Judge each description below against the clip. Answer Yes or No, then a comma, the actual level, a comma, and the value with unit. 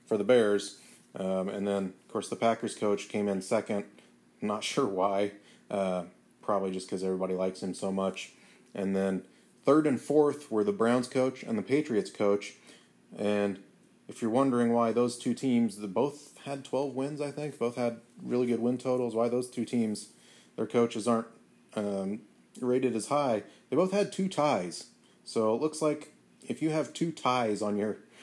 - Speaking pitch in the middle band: No, low, 115 Hz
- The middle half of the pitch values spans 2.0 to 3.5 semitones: No, average, 4.3 semitones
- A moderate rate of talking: Yes, average, 185 wpm